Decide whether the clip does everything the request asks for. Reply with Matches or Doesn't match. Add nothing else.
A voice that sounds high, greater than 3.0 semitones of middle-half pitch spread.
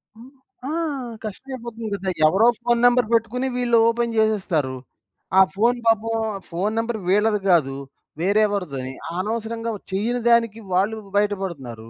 Matches